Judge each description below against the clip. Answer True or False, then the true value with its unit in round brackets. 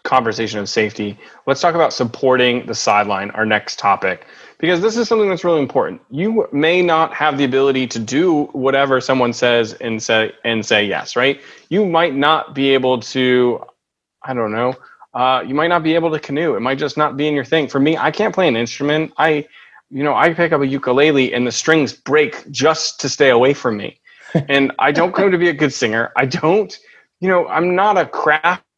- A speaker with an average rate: False (215 wpm)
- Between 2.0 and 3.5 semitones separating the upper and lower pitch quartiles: False (4.2 semitones)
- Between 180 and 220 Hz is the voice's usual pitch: False (140 Hz)